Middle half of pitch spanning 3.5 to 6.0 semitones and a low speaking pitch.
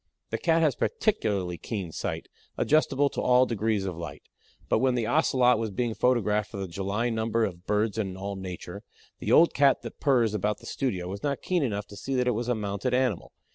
Yes: average, 4.2 semitones; low, 110 Hz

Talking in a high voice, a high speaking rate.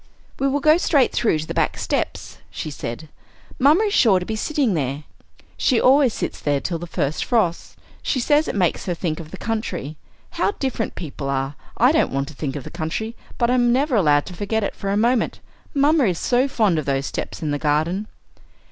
Yes: high, 200 Hz; fast, 215 wpm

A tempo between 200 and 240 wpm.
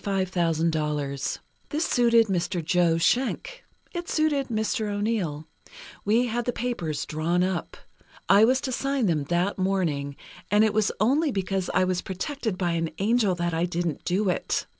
No: average, 155 wpm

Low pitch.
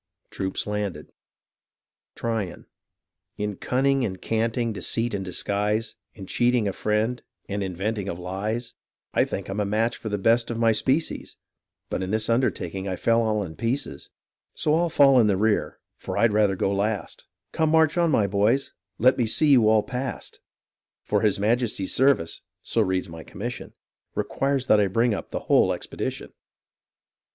Yes: low, 110 Hz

